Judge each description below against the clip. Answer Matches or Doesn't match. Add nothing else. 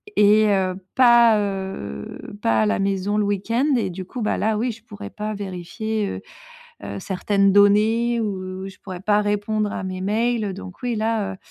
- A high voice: Matches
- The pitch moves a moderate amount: Doesn't match